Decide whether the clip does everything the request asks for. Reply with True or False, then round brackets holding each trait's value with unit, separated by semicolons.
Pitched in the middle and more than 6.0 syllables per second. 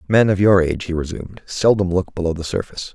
False (90 Hz; 6.6 syllables/s)